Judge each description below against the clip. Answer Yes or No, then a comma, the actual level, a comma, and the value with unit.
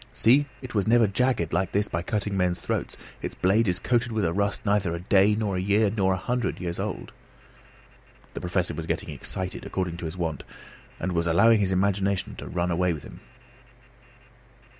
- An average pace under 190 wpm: No, average, 195 wpm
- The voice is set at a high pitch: No, very low, 95 Hz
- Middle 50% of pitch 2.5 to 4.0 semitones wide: Yes, average, 3.1 semitones